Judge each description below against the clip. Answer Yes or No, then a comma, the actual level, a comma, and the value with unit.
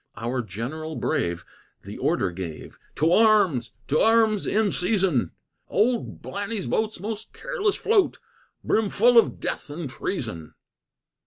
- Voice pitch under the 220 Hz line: Yes, high, 190 Hz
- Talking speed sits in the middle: No, slow, 130 wpm